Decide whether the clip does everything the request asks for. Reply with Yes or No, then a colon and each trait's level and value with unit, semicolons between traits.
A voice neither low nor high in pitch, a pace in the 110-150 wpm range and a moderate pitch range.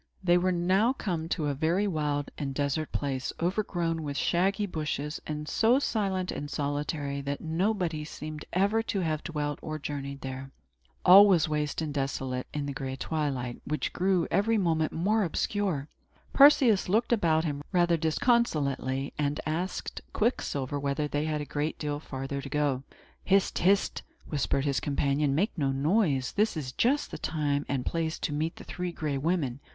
No: medium, 155 Hz; average, 170 wpm; average, 4.4 semitones